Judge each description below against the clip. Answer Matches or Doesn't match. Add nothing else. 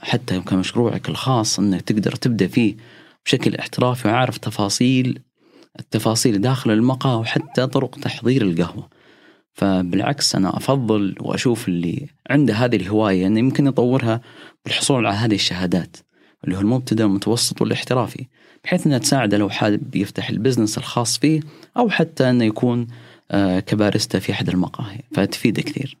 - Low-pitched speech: Matches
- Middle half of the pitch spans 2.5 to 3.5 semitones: Doesn't match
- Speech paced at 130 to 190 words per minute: Matches